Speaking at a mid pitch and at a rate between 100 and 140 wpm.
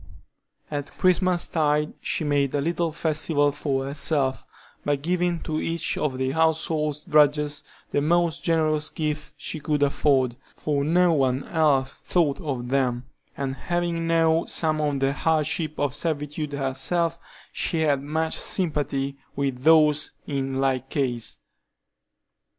Yes: medium, 150 Hz; slow, 135 wpm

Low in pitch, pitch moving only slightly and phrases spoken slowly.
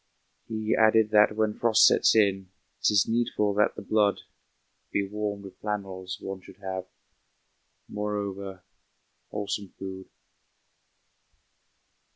Yes: low, 100 Hz; narrow, 1.6 semitones; slow, 110 wpm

